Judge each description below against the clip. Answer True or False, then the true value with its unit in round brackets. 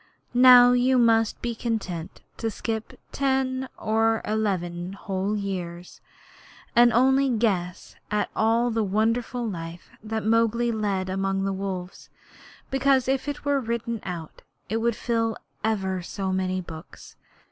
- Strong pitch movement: False (3.9 semitones)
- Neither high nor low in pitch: False (220 Hz)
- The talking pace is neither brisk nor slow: False (130 wpm)